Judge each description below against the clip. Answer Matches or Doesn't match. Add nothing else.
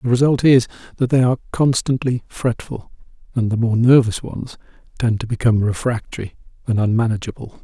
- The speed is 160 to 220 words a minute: Doesn't match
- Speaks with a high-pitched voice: Doesn't match